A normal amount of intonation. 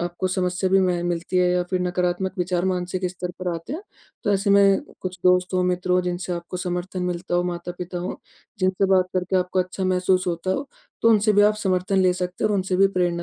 No: narrow, 1.0 semitones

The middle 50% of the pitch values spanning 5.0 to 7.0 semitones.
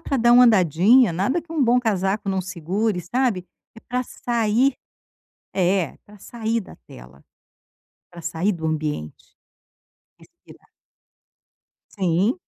Yes: wide, 5.4 semitones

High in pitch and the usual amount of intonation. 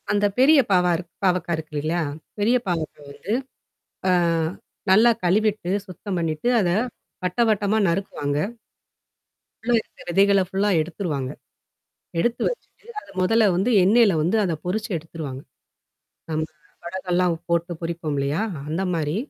No: medium, 180 Hz; average, 4.0 semitones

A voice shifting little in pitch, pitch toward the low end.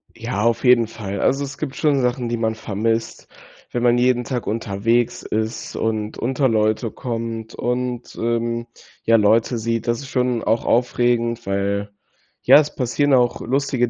Yes: narrow, 1.8 semitones; low, 115 Hz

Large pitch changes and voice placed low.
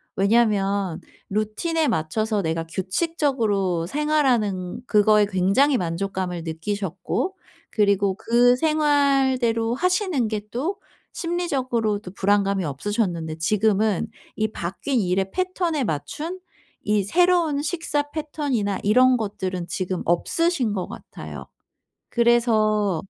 No: wide, 6.6 semitones; high, 215 Hz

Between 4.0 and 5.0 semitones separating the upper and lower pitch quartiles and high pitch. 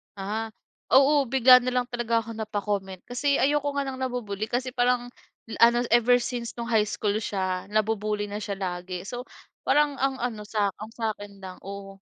No: average, 3.4 semitones; high, 225 Hz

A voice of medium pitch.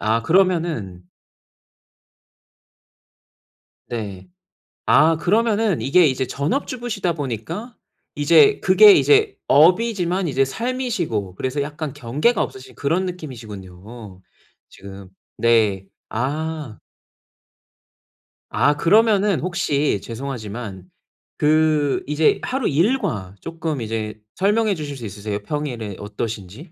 Yes: medium, 145 Hz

